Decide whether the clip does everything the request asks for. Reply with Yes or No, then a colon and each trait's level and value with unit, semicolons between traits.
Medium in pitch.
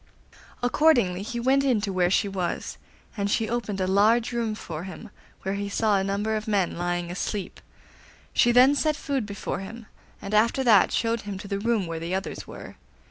No: high, 205 Hz